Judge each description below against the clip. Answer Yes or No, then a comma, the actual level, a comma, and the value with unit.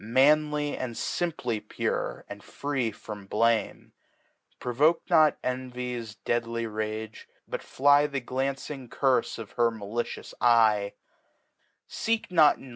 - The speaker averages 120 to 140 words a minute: Yes, slow, 135 wpm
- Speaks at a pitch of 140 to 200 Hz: No, low, 125 Hz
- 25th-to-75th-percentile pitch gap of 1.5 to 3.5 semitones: No, average, 4.1 semitones